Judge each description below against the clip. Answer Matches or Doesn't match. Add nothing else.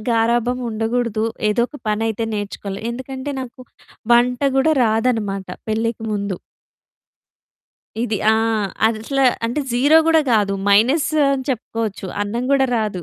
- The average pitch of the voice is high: Matches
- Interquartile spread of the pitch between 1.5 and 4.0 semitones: Matches